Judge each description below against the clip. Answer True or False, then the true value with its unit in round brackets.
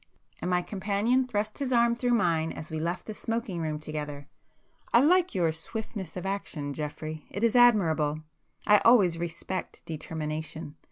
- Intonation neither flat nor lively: False (6.2 semitones)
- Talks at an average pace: True (155 wpm)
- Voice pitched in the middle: True (180 Hz)